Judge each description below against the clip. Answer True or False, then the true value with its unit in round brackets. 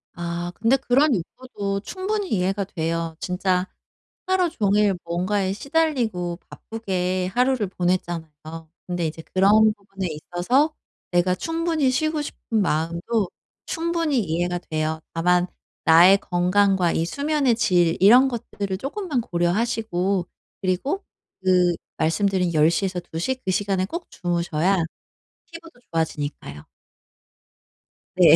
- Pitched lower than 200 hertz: True (190 Hz)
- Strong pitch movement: True (5.8 semitones)